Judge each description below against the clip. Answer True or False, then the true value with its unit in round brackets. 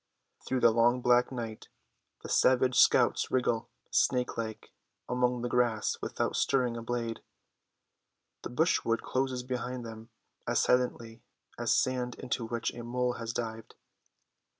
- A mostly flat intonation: True (1.5 semitones)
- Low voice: True (120 Hz)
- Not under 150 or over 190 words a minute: False (135 wpm)